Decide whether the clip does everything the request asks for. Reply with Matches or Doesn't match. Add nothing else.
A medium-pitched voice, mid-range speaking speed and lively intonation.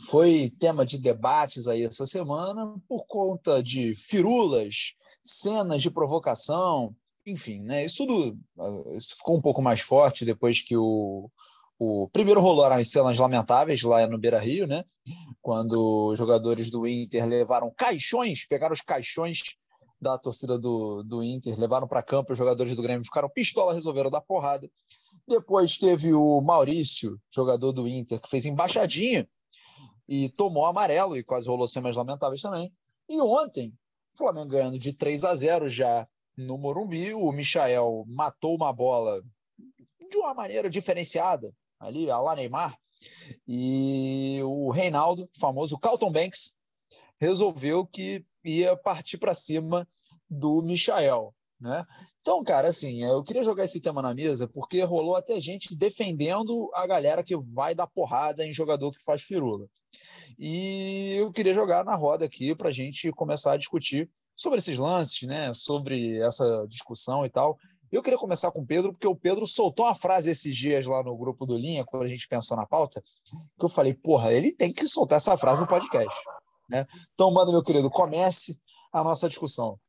Matches